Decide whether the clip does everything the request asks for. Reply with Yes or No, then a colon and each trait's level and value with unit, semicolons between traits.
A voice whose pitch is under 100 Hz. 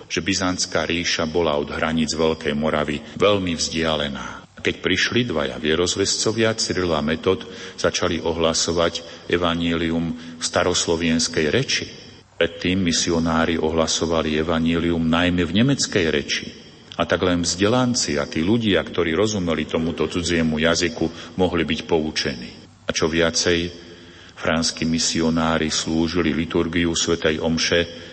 Yes: very low, 85 Hz